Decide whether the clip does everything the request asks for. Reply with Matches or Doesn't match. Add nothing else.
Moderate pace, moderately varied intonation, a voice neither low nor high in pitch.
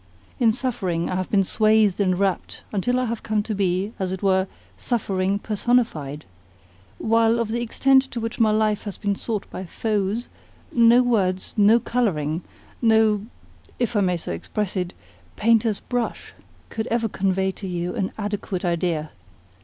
Doesn't match